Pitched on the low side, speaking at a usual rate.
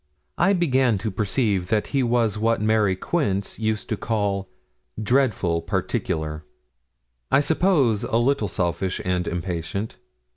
No: low, 105 Hz; slow, 125 wpm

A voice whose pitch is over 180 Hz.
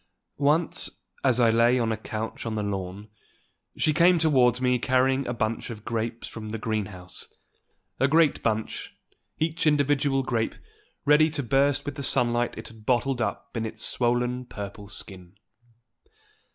No: low, 120 Hz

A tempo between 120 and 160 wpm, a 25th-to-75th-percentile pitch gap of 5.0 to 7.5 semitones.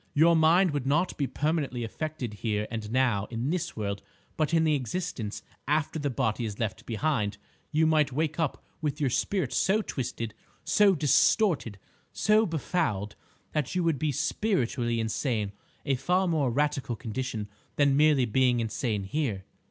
Yes: average, 155 wpm; wide, 5.6 semitones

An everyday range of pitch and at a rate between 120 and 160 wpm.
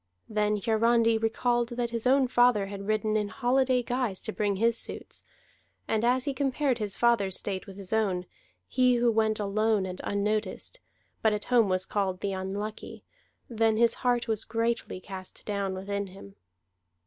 No: average, 3.1 semitones; average, 170 wpm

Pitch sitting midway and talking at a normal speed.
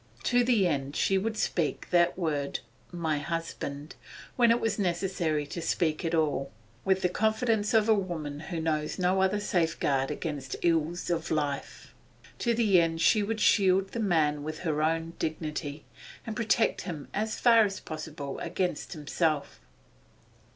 Yes: medium, 170 Hz; average, 165 wpm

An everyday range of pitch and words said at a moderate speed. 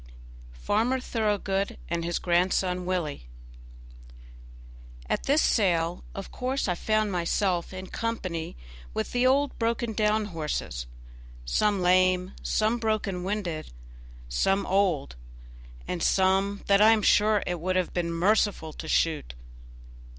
No: average, 3.8 semitones; slow, 130 wpm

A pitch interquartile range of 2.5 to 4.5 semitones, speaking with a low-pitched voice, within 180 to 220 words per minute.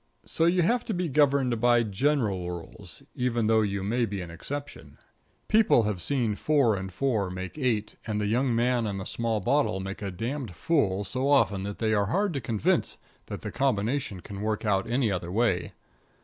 No: wide, 5.4 semitones; low, 115 Hz; average, 195 wpm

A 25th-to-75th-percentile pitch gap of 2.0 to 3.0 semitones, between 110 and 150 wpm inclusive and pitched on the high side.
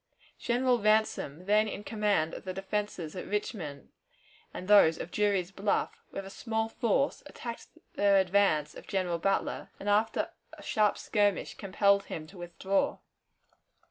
Yes: narrow, 2.5 semitones; average, 145 wpm; high, 200 Hz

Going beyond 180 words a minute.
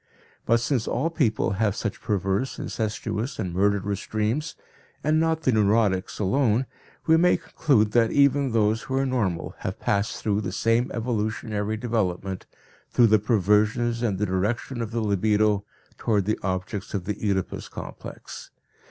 No: average, 150 wpm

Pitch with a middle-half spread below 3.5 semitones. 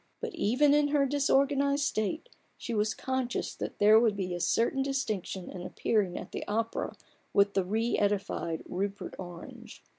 No: wide, 5.4 semitones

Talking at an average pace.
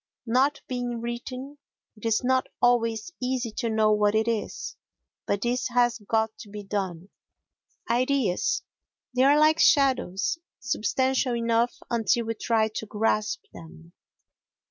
No: slow, 130 wpm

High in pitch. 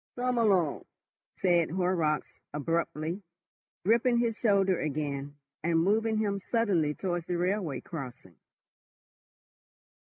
No: medium, 175 Hz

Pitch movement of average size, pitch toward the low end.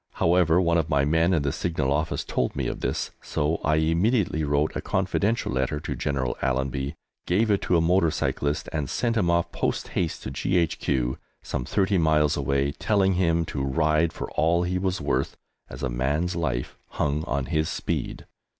Yes: average, 3.7 semitones; very low, 80 Hz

